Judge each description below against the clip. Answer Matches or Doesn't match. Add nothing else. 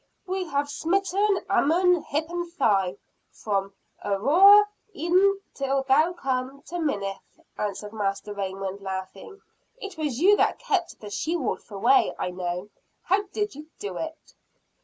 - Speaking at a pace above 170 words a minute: Doesn't match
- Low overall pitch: Doesn't match